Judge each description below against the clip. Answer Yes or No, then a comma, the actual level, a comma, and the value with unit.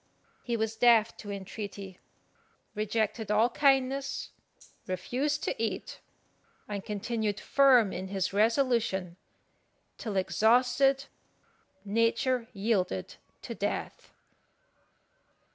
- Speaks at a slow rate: Yes, slow, 90 wpm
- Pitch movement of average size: Yes, average, 3.6 semitones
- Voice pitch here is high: Yes, high, 220 Hz